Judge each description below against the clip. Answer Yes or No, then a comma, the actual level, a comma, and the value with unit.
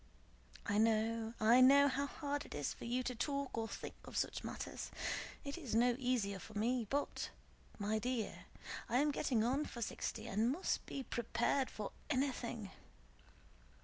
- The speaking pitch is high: Yes, high, 245 Hz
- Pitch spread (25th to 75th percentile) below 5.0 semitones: Yes, average, 3.8 semitones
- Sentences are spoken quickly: No, average, 165 wpm